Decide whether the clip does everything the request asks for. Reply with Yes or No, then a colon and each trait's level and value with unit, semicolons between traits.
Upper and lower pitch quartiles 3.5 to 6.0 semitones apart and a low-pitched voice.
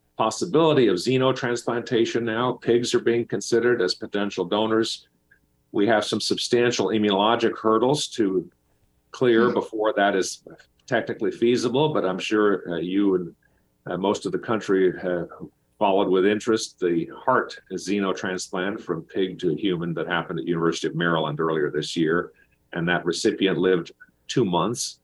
Yes: average, 4.3 semitones; low, 105 Hz